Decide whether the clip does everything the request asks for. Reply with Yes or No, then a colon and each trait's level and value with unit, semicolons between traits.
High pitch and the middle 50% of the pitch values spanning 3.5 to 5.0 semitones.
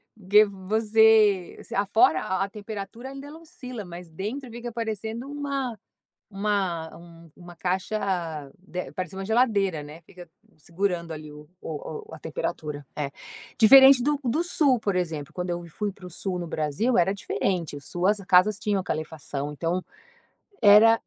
Yes: high, 195 Hz; average, 4.7 semitones